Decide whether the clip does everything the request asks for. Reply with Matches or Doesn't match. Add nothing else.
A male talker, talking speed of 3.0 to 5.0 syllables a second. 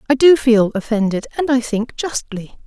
Doesn't match